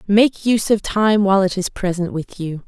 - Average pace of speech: No, fast, 225 wpm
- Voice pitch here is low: No, high, 200 Hz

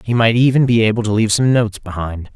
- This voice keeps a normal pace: No, fast, 255 wpm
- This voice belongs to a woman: No, male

